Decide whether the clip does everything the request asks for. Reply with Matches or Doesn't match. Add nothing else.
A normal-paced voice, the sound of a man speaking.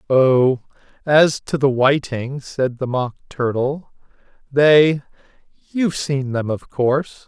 Doesn't match